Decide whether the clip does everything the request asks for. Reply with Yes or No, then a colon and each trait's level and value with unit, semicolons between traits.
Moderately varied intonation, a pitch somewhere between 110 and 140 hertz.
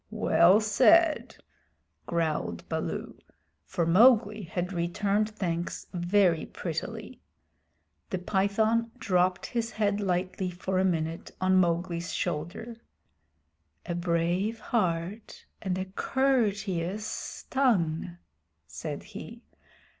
No: average, 3.8 semitones; medium, 185 Hz